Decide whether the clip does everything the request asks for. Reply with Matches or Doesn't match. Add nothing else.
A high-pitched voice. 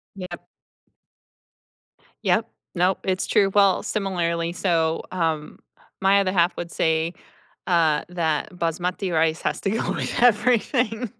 Doesn't match